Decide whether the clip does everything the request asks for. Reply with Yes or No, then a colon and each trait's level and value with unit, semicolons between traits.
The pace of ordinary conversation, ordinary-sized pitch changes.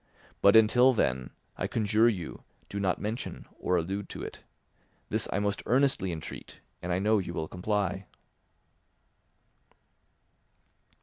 No: slow, 130 wpm; average, 3.4 semitones